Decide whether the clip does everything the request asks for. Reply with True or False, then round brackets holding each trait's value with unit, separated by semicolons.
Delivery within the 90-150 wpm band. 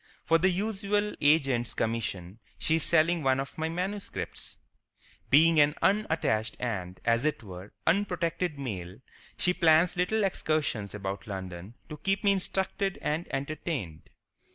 True (135 wpm)